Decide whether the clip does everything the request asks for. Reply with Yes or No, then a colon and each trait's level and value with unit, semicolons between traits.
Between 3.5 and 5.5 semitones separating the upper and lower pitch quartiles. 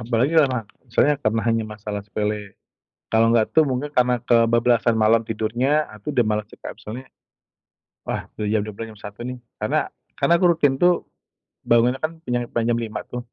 No: average, 2.7 semitones